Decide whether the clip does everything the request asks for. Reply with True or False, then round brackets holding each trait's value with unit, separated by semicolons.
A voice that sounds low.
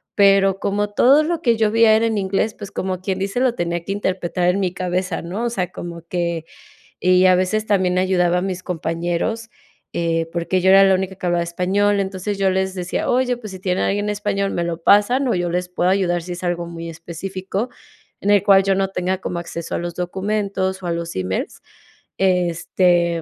False (185 Hz)